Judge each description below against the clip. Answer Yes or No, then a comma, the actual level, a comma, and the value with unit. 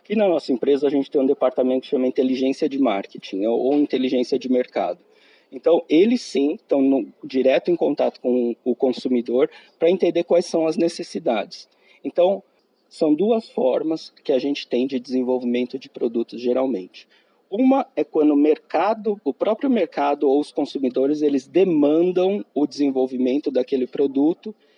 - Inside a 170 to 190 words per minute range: No, average, 155 wpm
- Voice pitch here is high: No, medium, 140 Hz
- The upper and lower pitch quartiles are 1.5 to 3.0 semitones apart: No, average, 4.6 semitones